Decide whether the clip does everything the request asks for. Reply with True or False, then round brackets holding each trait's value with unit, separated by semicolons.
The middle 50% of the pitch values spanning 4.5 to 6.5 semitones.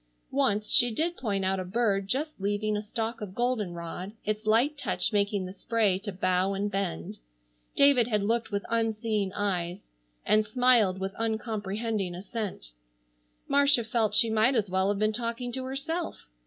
False (3.2 semitones)